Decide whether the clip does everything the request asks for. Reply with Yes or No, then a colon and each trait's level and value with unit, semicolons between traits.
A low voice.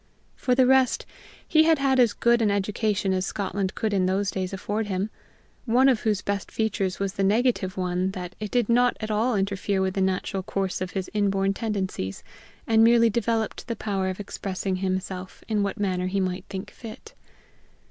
No: high, 200 Hz